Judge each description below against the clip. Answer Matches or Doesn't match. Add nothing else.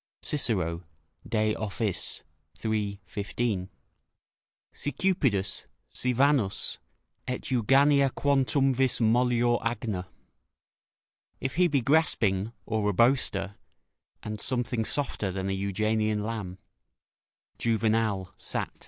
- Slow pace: Matches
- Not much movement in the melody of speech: Doesn't match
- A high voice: Doesn't match